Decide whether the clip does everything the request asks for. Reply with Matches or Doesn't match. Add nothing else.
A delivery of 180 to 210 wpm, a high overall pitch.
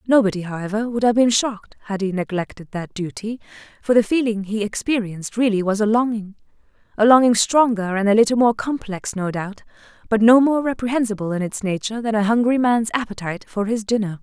Matches